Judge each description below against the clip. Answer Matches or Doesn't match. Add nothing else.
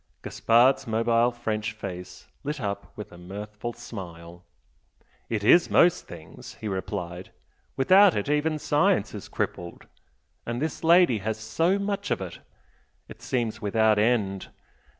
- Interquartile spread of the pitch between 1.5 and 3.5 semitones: Doesn't match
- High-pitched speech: Doesn't match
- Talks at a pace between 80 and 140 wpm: Matches